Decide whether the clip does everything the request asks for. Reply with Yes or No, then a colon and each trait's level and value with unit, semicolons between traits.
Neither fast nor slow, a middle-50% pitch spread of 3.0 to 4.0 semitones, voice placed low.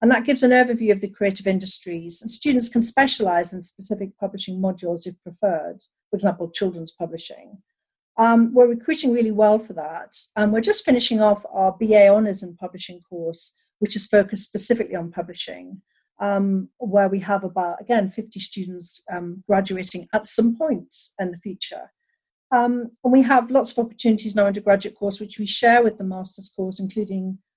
No: average, 180 wpm; average, 3.5 semitones; high, 205 Hz